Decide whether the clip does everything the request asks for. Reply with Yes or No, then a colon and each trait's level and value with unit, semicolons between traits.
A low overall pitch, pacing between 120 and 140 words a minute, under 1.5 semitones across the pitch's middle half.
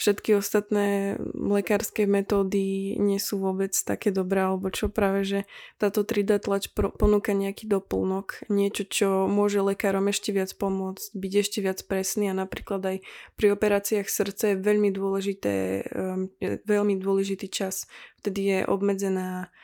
No: high, 200 Hz; average, 135 wpm; narrow, 1.0 semitones